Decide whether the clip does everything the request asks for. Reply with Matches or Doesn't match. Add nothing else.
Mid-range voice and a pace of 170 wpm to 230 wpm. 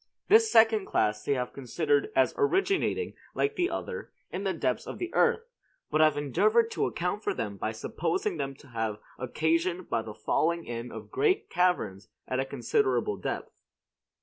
Matches